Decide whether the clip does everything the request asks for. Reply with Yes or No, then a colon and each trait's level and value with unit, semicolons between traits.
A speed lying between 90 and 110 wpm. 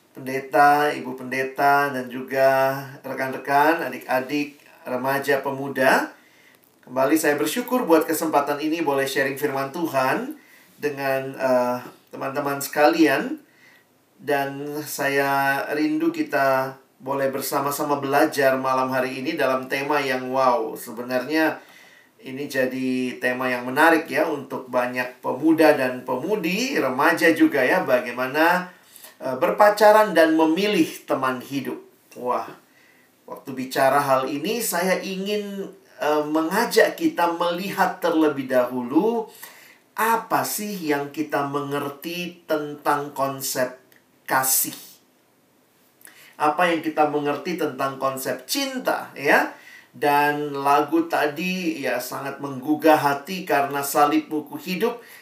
Yes: average, 105 wpm